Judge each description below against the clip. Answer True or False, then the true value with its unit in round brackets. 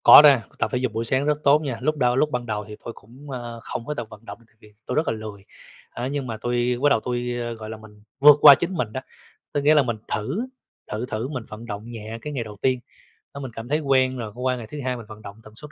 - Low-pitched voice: True (125 Hz)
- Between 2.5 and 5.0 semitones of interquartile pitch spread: True (3.9 semitones)